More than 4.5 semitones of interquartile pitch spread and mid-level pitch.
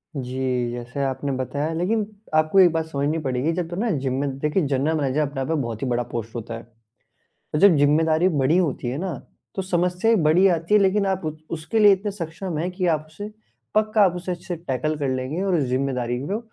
Yes: wide, 5.5 semitones; medium, 155 Hz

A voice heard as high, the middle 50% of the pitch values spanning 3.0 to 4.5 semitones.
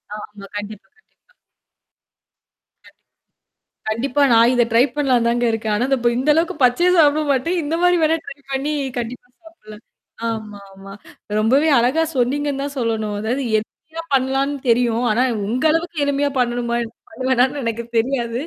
Yes: very high, 250 Hz; average, 3.9 semitones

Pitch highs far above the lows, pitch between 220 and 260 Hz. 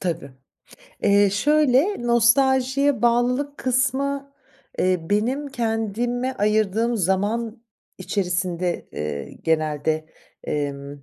Yes: wide, 6.0 semitones; high, 225 Hz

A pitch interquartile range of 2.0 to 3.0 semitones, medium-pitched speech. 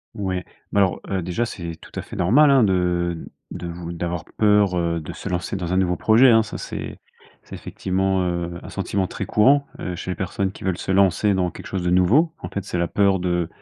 No: narrow, 2.5 semitones; very low, 95 Hz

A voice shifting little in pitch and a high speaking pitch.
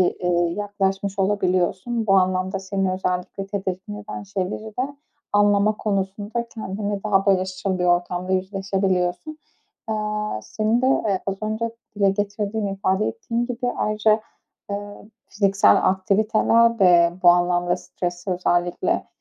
Yes: narrow, 2.3 semitones; high, 195 Hz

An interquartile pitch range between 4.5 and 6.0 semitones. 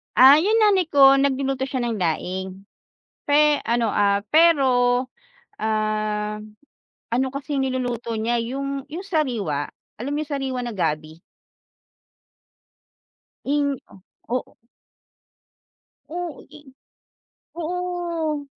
Yes: average, 5.3 semitones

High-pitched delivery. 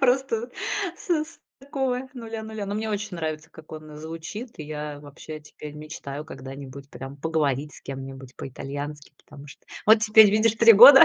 No: medium, 160 Hz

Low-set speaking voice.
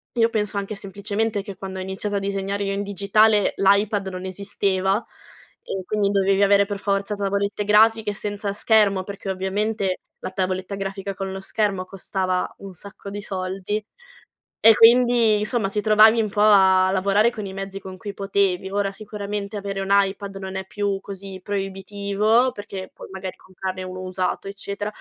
No: high, 200 Hz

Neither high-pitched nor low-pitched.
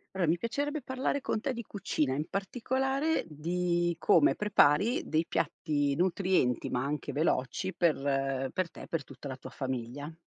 Yes: medium, 170 Hz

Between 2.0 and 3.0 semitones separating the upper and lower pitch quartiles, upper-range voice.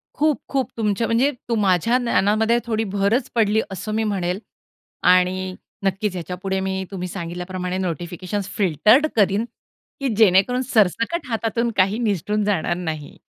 No: average, 3.6 semitones; high, 200 Hz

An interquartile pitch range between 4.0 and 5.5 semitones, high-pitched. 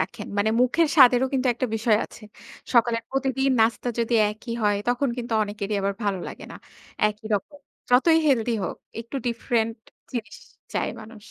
No: average, 3.0 semitones; high, 235 Hz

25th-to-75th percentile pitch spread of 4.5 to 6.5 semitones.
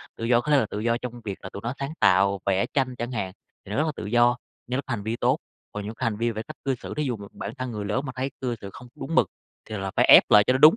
No: average, 3.7 semitones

